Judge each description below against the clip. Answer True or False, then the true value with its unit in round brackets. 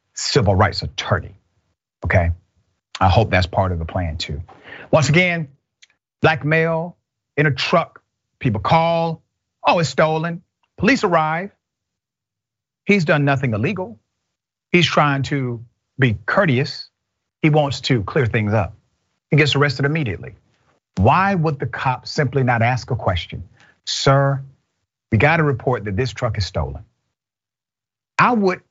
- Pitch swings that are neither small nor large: False (6.8 semitones)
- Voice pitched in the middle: False (130 Hz)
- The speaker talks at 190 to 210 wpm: False (140 wpm)